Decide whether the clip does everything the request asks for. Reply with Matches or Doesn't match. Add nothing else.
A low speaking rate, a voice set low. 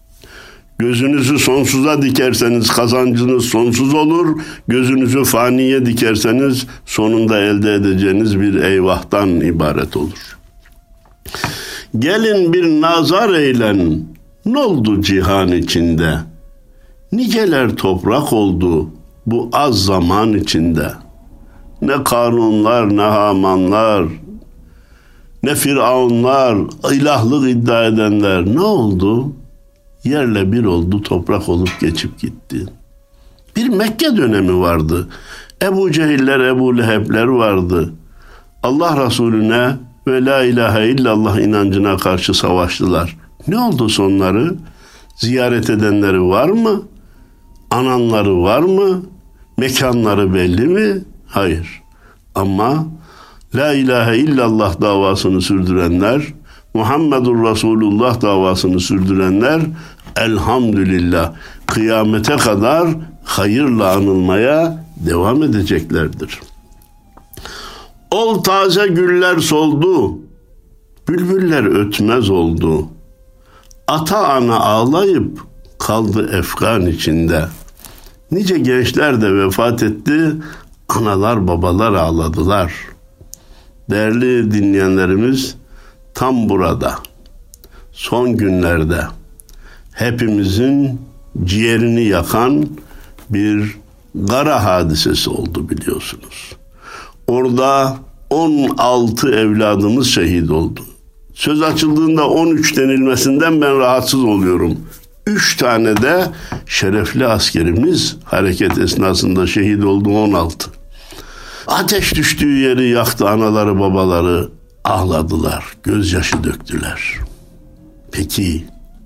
Matches